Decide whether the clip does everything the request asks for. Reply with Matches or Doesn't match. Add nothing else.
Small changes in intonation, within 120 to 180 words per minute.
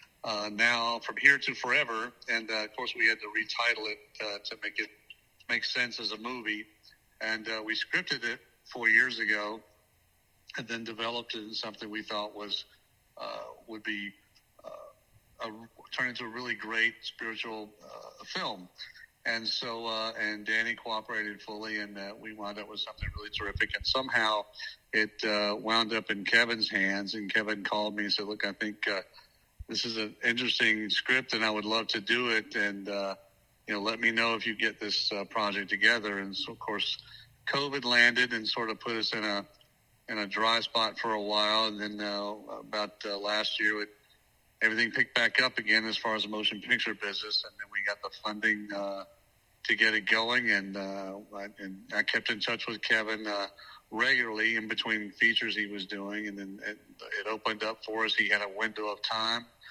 Doesn't match